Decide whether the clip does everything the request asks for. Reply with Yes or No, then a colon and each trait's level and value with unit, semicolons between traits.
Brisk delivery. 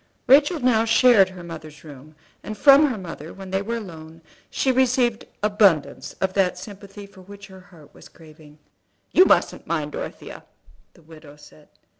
No: average, 170 wpm